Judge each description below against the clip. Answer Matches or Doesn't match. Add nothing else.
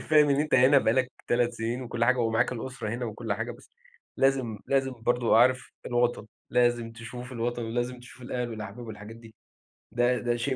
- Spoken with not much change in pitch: Matches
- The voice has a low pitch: Matches